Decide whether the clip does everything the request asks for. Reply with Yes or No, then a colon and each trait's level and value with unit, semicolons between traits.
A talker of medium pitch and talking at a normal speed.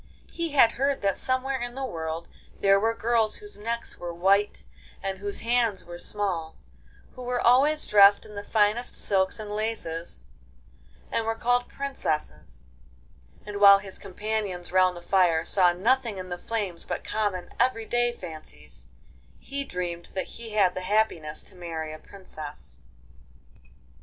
No: high, 205 Hz; average, 150 wpm